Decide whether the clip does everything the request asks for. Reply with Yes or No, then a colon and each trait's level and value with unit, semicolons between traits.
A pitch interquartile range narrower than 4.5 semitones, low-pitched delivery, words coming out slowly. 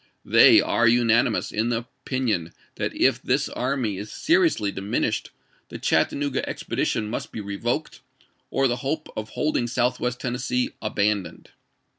Yes: average, 3.3 semitones; low, 120 Hz; slow, 130 wpm